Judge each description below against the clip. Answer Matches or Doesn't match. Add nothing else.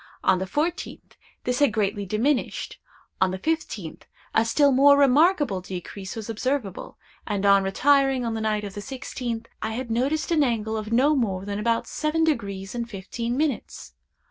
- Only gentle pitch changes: Doesn't match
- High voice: Matches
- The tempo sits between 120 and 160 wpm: Doesn't match